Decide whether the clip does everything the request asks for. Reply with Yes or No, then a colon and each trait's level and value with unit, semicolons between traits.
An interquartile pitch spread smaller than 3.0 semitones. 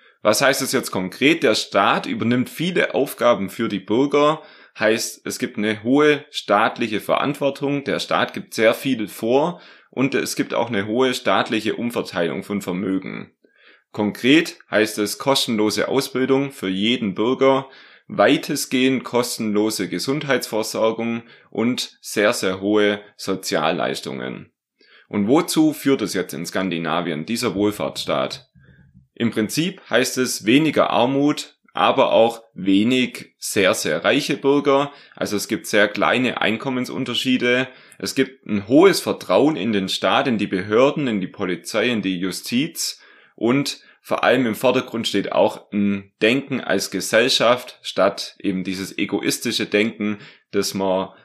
No: average, 5.1 semitones